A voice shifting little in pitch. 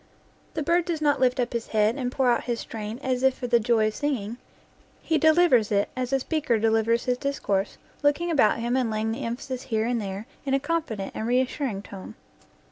No: average, 3.9 semitones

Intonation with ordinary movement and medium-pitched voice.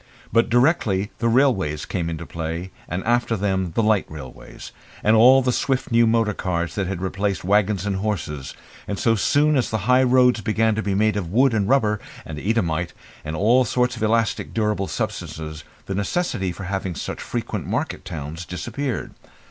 No: average, 4.6 semitones; low, 105 Hz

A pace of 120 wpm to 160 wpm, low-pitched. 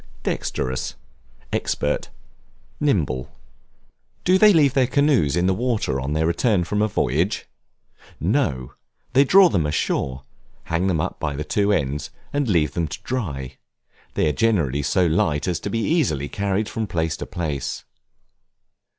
Yes: average, 150 wpm; very low, 85 Hz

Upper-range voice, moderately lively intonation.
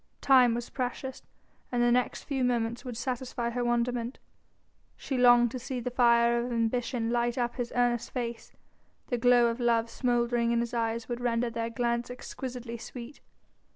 No: high, 240 Hz; narrow, 1.0 semitones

